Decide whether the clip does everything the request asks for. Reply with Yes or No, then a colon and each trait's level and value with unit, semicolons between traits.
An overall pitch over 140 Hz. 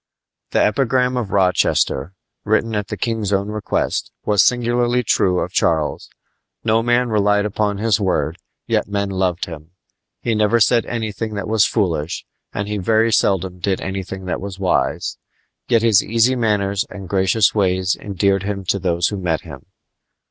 No: low, 100 Hz